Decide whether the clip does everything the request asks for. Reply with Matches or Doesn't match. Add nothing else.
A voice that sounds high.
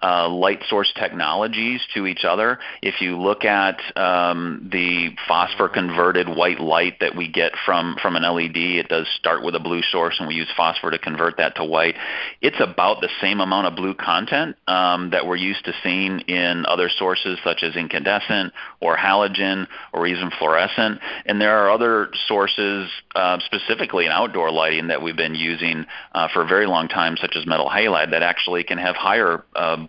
Doesn't match